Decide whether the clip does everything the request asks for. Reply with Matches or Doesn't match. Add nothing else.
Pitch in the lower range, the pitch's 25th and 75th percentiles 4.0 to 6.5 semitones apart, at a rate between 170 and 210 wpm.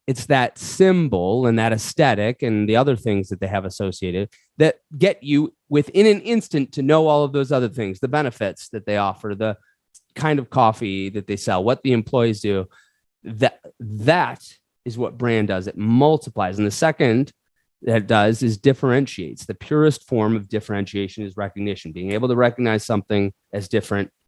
Matches